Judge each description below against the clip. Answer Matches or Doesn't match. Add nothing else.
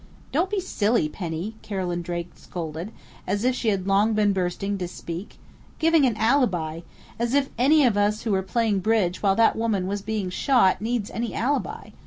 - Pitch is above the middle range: Matches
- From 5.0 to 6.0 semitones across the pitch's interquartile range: Doesn't match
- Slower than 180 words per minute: Doesn't match